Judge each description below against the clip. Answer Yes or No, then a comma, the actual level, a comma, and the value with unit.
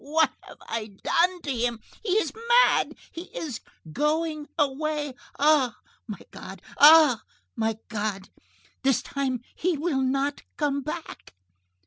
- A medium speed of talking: No, slow, 130 wpm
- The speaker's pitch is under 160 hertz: No, very high, 285 Hz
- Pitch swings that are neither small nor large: Yes, average, 4.4 semitones